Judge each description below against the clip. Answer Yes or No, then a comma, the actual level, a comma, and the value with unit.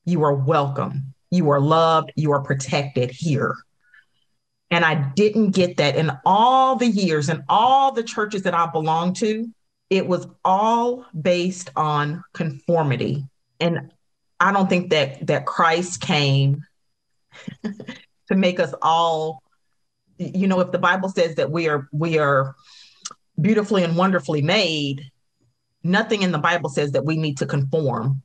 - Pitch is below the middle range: No, medium, 165 Hz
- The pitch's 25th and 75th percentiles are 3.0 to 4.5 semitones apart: Yes, average, 4.1 semitones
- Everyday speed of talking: Yes, average, 150 wpm